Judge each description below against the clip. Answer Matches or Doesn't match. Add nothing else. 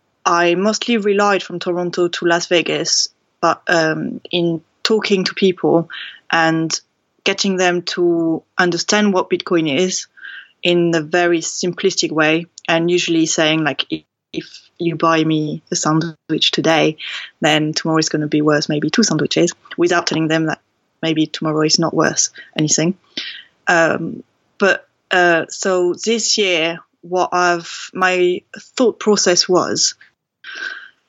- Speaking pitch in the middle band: Matches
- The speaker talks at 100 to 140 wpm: Matches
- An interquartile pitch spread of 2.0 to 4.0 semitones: Matches